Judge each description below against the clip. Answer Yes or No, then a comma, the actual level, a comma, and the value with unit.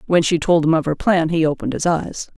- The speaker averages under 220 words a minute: No, fast, 275 wpm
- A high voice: No, medium, 165 Hz